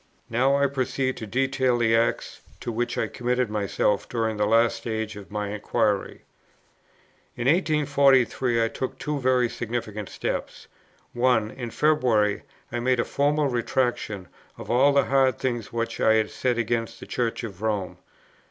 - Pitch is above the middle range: No, low, 120 Hz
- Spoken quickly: No, average, 160 wpm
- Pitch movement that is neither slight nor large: Yes, average, 3.0 semitones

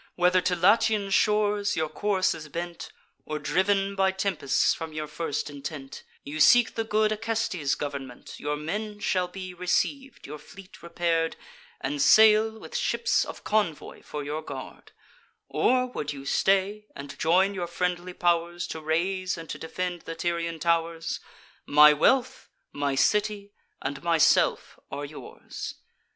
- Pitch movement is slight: No, average, 4.8 semitones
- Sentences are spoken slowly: No, average, 145 wpm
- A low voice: No, medium, 175 Hz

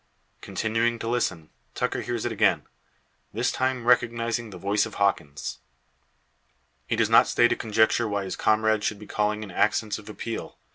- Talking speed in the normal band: Yes, average, 170 wpm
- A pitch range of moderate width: No, narrow, 2.2 semitones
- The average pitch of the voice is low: Yes, low, 110 Hz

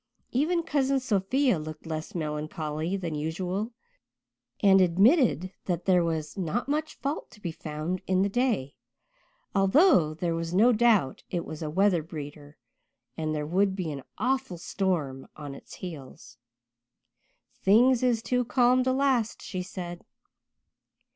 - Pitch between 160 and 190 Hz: Yes, medium, 185 Hz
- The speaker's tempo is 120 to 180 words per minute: Yes, average, 140 wpm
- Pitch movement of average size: No, wide, 7.3 semitones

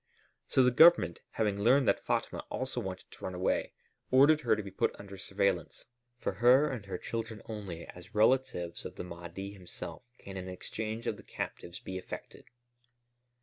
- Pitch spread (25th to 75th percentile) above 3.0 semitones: Yes, average, 4.6 semitones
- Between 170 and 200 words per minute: Yes, average, 175 wpm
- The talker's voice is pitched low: Yes, low, 100 Hz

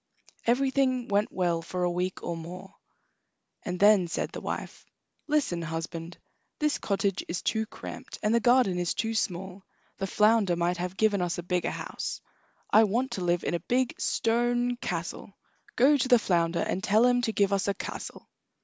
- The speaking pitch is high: Yes, high, 200 Hz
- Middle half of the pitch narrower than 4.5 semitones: No, average, 5.0 semitones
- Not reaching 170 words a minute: No, average, 180 wpm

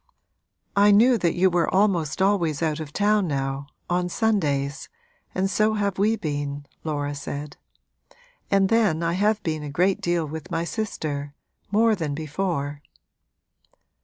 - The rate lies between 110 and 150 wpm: Yes, average, 145 wpm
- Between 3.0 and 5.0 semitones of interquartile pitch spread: No, wide, 5.5 semitones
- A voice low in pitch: No, medium, 170 Hz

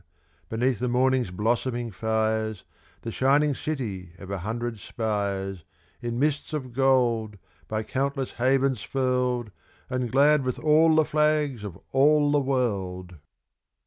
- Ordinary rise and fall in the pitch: Yes, average, 3.8 semitones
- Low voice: Yes, low, 125 Hz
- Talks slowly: Yes, slow, 130 wpm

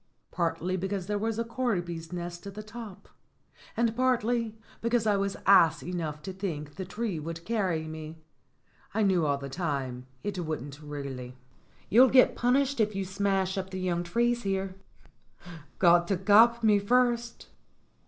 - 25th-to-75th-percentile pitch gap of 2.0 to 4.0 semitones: No, average, 5.0 semitones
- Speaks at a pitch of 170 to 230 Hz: Yes, high, 190 Hz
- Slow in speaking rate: No, average, 160 wpm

